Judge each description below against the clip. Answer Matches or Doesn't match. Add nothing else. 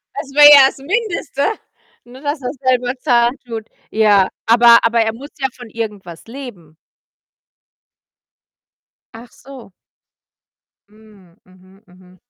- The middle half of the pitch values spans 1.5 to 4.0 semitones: Doesn't match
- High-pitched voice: Matches